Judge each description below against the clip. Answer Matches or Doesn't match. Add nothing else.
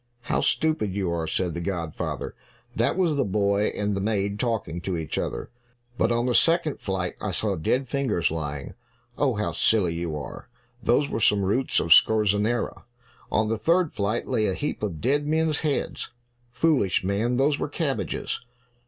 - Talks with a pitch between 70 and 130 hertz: Matches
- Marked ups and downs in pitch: Matches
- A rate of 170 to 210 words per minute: Matches